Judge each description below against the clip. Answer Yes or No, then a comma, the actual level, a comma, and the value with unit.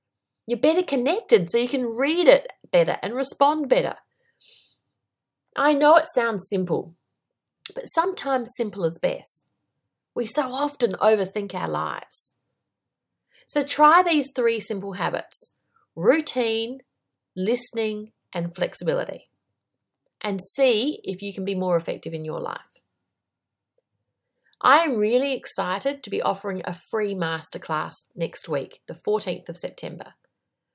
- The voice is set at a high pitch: Yes, high, 235 Hz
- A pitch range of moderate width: No, wide, 6.8 semitones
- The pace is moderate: No, slow, 125 wpm